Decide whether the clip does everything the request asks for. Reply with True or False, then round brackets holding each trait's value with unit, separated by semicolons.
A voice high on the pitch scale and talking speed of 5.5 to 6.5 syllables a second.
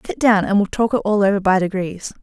True (200 Hz; 5.9 syllables/s)